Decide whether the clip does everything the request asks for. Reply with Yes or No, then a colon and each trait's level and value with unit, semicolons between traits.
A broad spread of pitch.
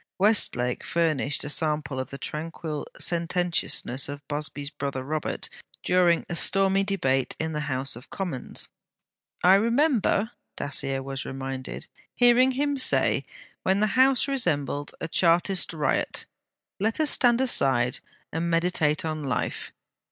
Yes: wide, 5.9 semitones